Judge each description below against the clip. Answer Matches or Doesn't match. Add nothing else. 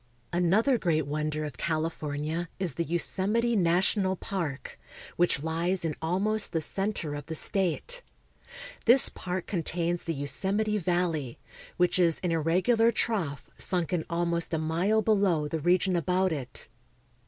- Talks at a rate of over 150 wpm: Doesn't match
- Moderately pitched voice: Matches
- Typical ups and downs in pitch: Matches